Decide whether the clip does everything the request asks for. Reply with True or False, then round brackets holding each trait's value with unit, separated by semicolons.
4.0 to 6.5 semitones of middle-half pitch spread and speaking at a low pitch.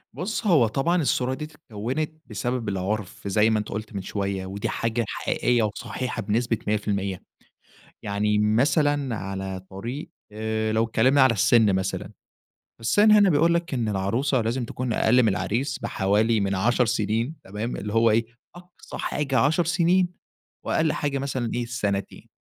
True (4.7 semitones; 115 Hz)